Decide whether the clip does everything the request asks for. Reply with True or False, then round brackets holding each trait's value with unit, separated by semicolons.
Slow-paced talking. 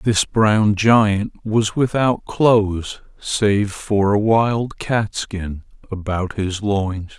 True (125 wpm)